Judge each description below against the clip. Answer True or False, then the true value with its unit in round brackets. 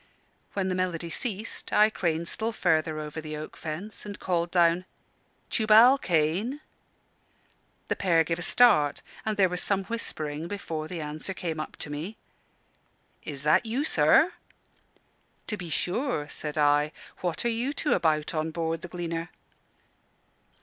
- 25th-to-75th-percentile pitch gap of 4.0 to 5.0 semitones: True (4.6 semitones)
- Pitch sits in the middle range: True (170 Hz)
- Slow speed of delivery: False (150 wpm)